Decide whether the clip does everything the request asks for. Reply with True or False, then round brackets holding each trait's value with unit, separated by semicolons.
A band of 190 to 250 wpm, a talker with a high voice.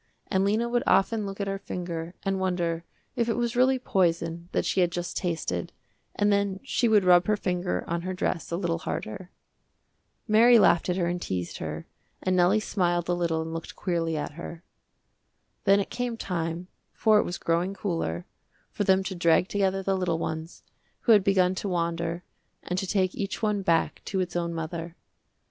False (195 wpm; 180 Hz)